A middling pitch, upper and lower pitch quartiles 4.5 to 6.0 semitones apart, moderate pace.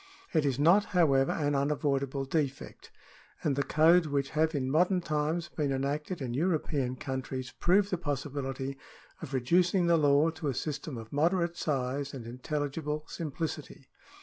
No: medium, 145 Hz; average, 3.2 semitones; average, 150 wpm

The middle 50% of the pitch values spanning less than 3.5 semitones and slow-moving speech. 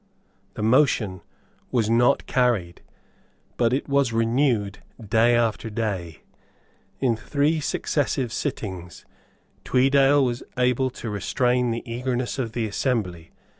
Yes: average, 3.1 semitones; slow, 115 wpm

